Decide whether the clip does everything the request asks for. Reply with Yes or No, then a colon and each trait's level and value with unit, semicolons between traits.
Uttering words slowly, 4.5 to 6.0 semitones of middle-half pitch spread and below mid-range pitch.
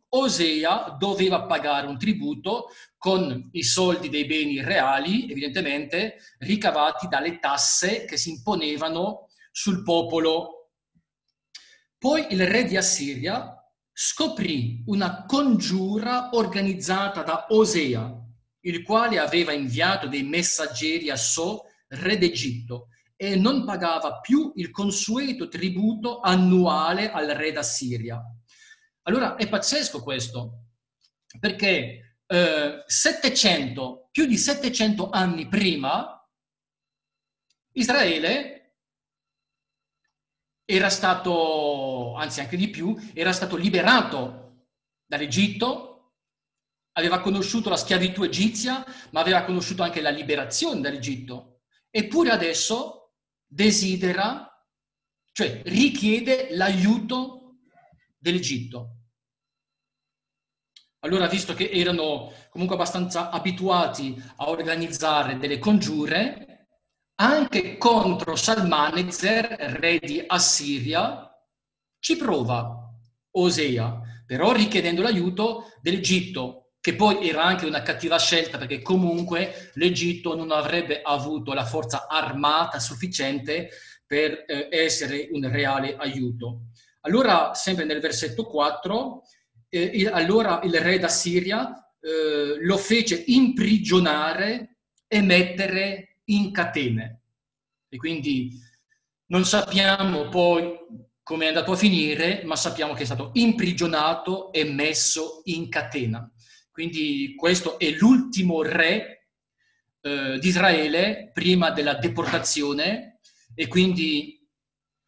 No: slow, 100 wpm; wide, 5.6 semitones; medium, 170 Hz